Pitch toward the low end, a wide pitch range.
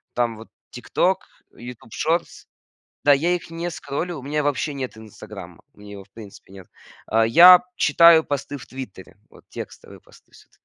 Yes: low, 130 Hz; wide, 6.8 semitones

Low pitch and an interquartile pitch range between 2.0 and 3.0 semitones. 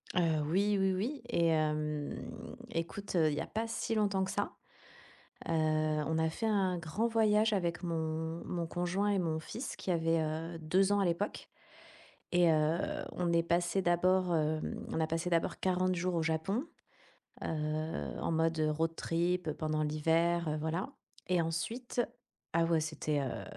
No: medium, 170 Hz; average, 2.7 semitones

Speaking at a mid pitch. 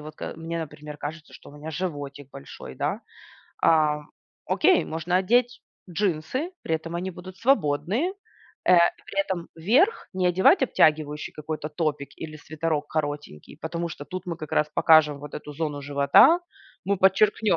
Yes: medium, 160 Hz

